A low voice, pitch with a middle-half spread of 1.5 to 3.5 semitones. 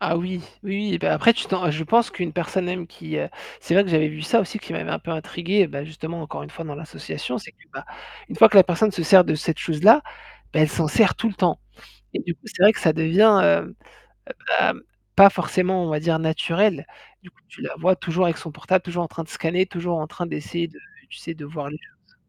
No: medium, 170 Hz; average, 3.0 semitones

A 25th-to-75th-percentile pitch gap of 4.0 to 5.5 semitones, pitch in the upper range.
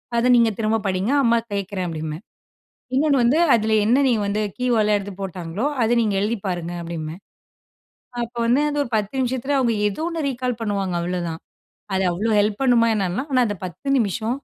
Yes: average, 4.5 semitones; high, 215 Hz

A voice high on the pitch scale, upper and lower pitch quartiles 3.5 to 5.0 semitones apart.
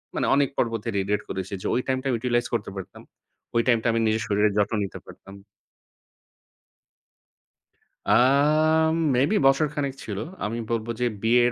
No: low, 120 Hz; average, 4.1 semitones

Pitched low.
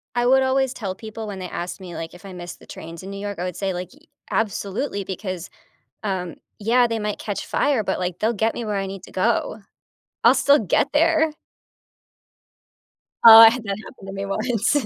No: high, 210 Hz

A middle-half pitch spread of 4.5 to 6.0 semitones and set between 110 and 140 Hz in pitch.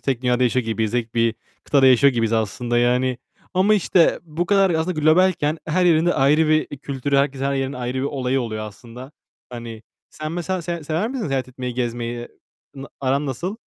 Yes: average, 4.8 semitones; low, 135 Hz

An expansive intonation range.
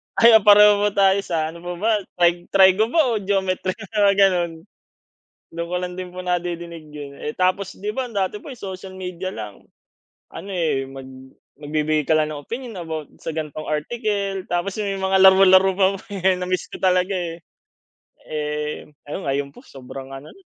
No: average, 4.0 semitones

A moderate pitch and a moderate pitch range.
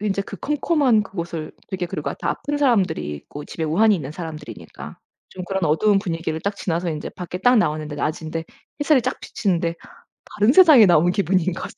Yes: medium, 180 Hz; average, 4.9 semitones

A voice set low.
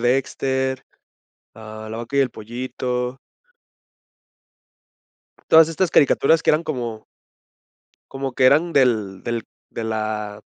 Yes: low, 125 Hz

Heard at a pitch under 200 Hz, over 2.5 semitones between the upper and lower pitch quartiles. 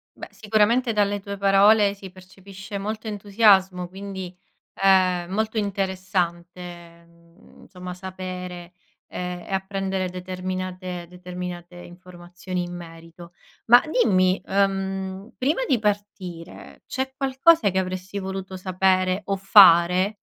No: high, 190 Hz; narrow, 1.9 semitones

